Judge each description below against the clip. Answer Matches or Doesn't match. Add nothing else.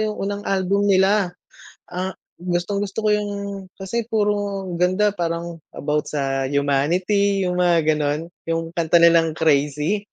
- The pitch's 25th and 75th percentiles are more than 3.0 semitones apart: Matches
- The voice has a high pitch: Doesn't match